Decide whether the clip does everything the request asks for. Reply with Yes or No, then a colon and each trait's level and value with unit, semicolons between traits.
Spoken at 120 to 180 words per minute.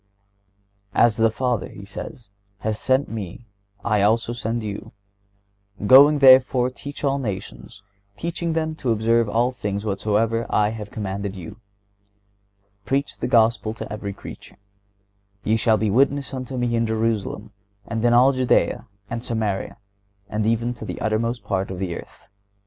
Yes: average, 150 wpm